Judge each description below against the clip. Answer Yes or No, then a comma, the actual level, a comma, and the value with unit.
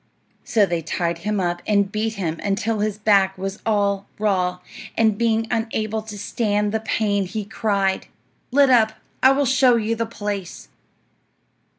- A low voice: No, high, 210 Hz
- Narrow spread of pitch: Yes, narrow, 2.3 semitones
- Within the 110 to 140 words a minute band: No, average, 160 wpm